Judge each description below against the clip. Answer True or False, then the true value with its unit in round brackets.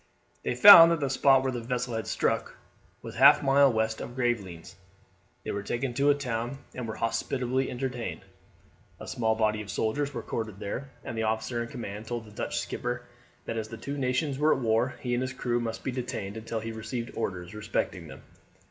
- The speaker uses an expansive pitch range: False (2.9 semitones)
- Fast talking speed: True (210 wpm)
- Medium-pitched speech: False (120 Hz)